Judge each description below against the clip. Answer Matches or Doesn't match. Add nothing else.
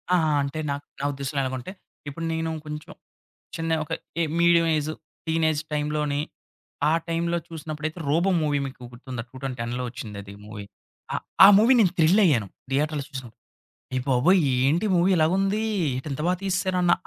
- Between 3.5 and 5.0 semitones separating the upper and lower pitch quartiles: Matches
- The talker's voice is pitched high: Doesn't match